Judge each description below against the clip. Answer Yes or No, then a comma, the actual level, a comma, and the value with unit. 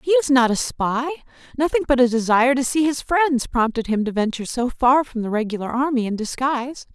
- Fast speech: Yes, fast, 215 wpm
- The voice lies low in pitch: No, very high, 255 Hz